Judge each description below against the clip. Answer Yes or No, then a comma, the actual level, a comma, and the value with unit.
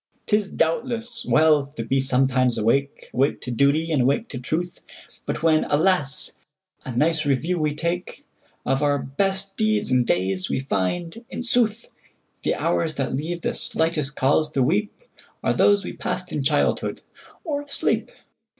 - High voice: No, medium, 155 Hz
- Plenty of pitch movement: Yes, wide, 6.0 semitones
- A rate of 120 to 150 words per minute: Yes, average, 145 wpm